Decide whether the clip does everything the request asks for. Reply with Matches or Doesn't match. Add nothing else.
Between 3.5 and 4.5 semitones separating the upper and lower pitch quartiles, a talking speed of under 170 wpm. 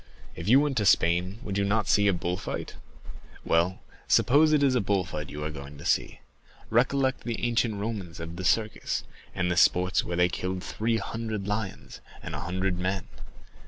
Doesn't match